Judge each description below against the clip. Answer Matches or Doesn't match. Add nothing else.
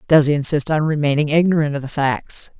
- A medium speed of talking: Doesn't match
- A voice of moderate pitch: Matches